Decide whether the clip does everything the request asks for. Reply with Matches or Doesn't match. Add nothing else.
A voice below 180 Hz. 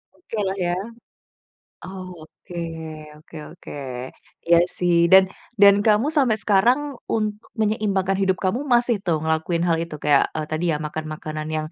Doesn't match